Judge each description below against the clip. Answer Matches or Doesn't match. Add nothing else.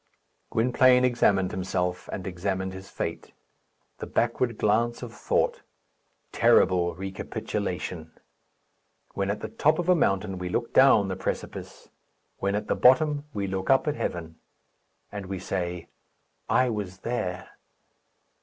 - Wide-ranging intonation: Doesn't match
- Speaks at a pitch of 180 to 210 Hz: Doesn't match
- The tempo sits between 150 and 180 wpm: Doesn't match